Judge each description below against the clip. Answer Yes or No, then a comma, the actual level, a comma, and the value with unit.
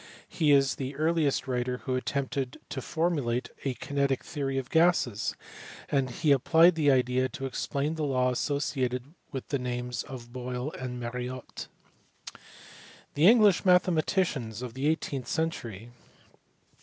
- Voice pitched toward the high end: No, low, 135 Hz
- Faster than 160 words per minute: No, slow, 135 wpm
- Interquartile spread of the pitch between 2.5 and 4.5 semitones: Yes, average, 3.3 semitones